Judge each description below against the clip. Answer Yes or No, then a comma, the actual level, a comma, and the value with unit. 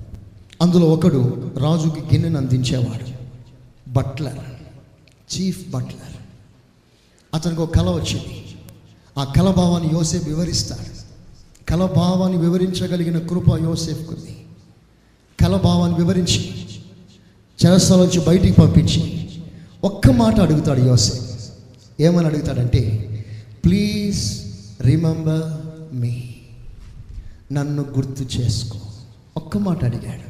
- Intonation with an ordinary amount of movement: No, wide, 6.2 semitones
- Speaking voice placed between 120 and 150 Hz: Yes, low, 135 Hz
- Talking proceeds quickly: No, average, 80 wpm